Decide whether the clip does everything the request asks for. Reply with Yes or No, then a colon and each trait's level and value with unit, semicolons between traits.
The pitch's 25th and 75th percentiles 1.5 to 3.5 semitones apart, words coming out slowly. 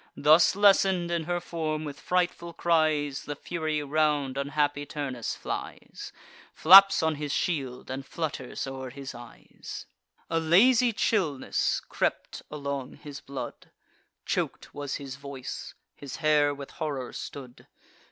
Yes: average, 3.2 semitones; slow, 130 wpm